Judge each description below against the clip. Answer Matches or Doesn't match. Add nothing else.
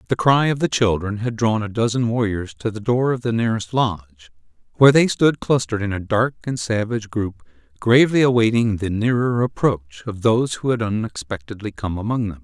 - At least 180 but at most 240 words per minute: Matches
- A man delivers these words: Matches